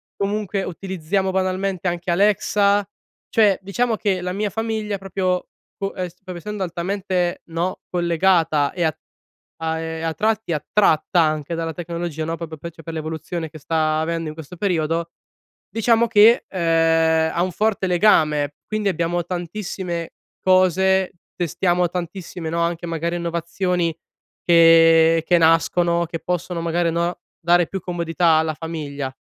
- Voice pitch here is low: No, medium, 175 Hz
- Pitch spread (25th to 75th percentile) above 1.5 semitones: Yes, narrow, 2.6 semitones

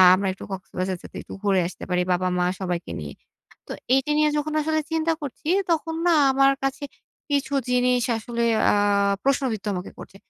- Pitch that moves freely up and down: Yes, wide, 7.5 semitones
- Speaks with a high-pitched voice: Yes, high, 245 Hz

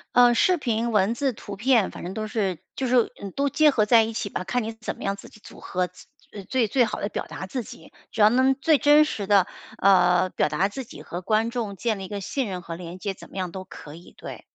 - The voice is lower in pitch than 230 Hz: Yes, high, 215 Hz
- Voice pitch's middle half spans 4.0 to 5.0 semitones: Yes, average, 4.5 semitones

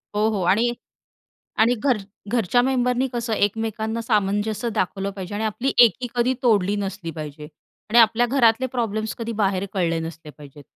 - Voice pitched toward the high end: Yes, high, 220 Hz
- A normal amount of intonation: Yes, average, 3.6 semitones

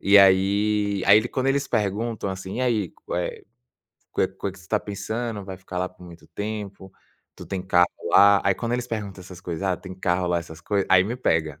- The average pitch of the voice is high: No, low, 100 Hz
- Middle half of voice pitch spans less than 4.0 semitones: Yes, narrow, 2.5 semitones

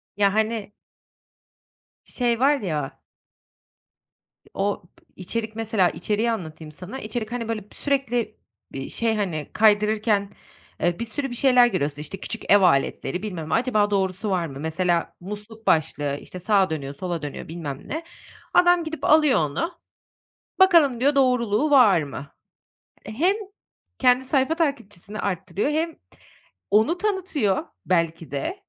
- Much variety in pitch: Yes, wide, 6.3 semitones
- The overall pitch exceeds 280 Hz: No, high, 210 Hz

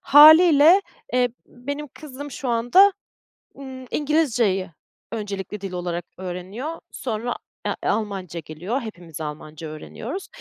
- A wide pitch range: Yes, wide, 7.8 semitones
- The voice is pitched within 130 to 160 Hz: No, high, 230 Hz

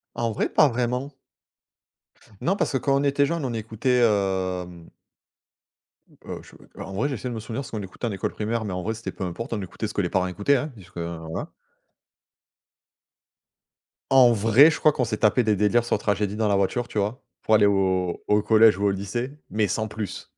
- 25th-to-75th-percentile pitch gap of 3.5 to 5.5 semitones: Yes, average, 3.8 semitones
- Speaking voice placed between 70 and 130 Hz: Yes, low, 110 Hz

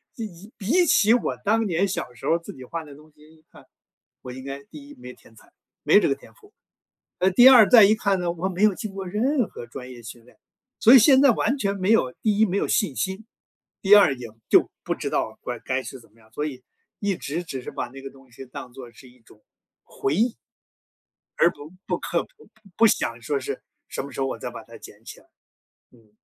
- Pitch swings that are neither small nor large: No, wide, 8.7 semitones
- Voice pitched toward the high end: No, medium, 170 Hz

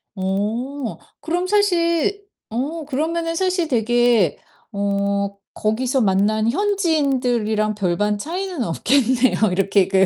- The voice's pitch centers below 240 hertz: No, high, 245 Hz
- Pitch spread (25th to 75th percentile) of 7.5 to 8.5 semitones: Yes, wide, 8.0 semitones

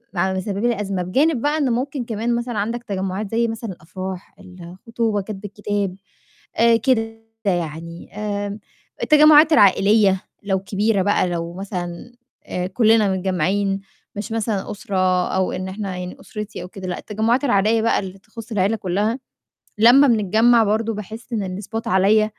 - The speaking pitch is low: No, high, 205 Hz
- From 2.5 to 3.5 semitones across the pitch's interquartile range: Yes, average, 3.2 semitones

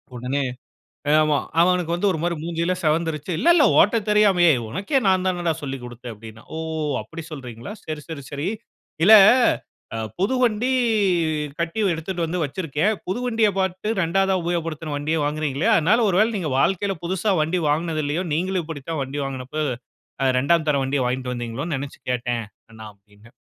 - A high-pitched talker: No, medium, 160 Hz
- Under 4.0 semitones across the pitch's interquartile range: No, average, 5.0 semitones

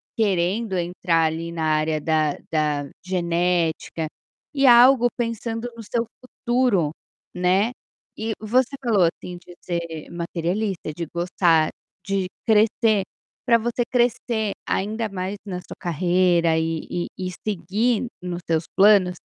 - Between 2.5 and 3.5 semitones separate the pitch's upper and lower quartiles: No, average, 4.7 semitones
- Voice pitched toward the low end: No, medium, 185 Hz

